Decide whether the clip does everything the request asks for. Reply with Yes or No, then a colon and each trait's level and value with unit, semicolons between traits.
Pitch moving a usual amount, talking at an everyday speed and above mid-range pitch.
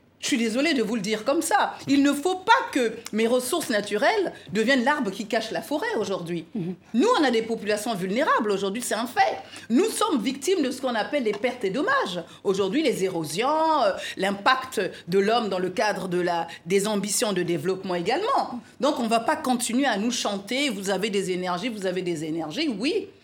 No: wide, 5.9 semitones; average, 205 wpm; high, 230 Hz